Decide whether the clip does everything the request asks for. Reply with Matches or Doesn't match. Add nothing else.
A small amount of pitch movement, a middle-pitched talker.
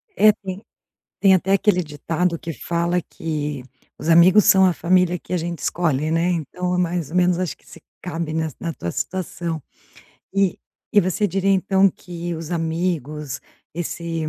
Matches